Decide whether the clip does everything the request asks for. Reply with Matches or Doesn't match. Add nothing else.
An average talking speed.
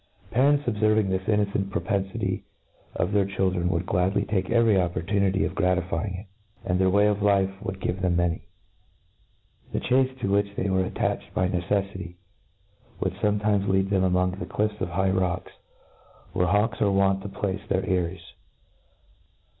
Matches